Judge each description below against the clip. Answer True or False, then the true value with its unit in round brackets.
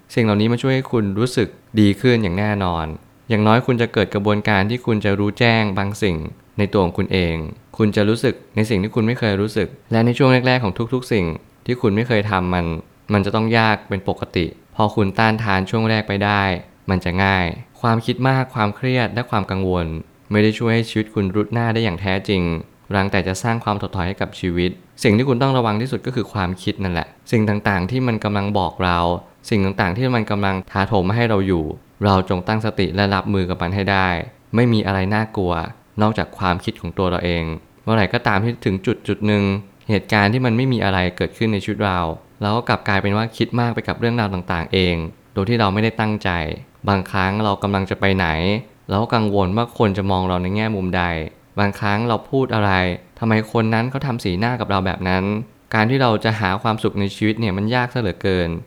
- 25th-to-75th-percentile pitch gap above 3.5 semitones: False (3.2 semitones)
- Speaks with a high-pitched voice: False (105 Hz)